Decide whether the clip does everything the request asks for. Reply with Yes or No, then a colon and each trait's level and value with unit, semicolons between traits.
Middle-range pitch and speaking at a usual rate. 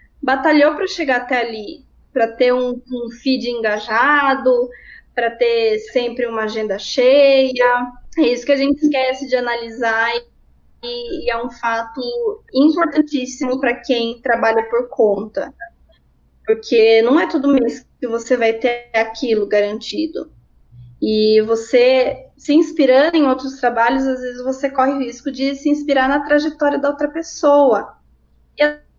No: very high, 255 Hz; average, 145 wpm